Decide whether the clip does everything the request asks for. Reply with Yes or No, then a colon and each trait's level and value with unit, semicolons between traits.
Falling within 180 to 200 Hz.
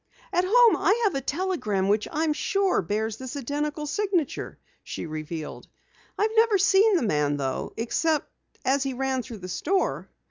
No: very high, 285 Hz